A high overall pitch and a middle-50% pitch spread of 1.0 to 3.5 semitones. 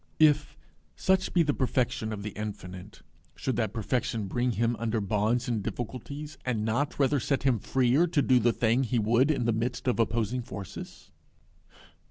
No: low, 120 Hz; average, 3.2 semitones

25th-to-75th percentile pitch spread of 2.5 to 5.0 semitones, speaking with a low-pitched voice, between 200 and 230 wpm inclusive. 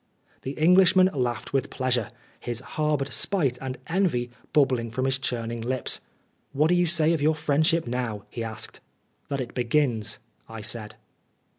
No: average, 4.5 semitones; low, 130 Hz; average, 160 wpm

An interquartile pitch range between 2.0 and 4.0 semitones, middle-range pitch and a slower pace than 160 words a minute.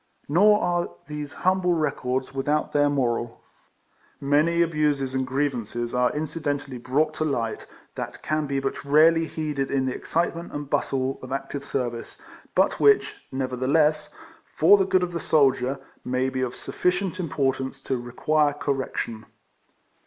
Yes: average, 3.2 semitones; medium, 145 Hz; average, 150 wpm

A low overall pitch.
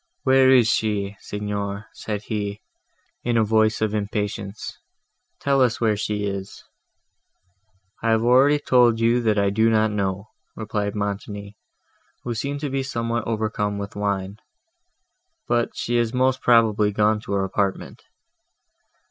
Yes: low, 110 Hz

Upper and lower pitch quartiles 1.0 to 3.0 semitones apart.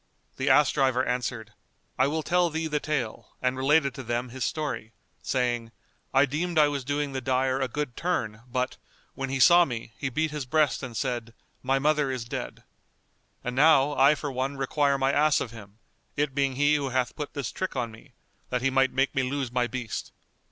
Yes: average, 2.7 semitones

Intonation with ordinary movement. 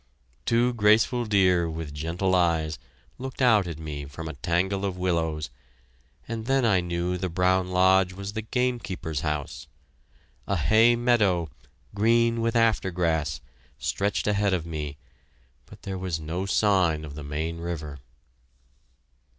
Yes: average, 4.5 semitones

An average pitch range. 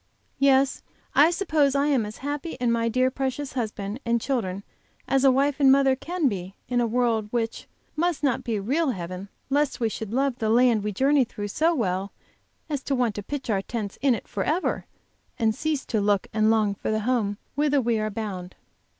Yes: average, 4.6 semitones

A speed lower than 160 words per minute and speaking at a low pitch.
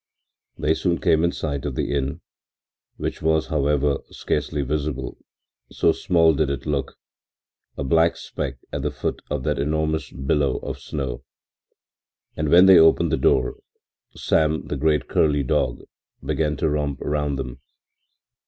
Yes: average, 150 wpm; very low, 75 Hz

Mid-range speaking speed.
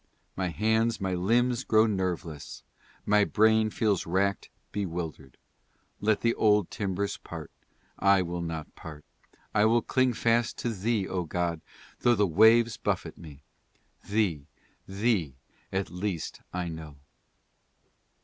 No: slow, 130 wpm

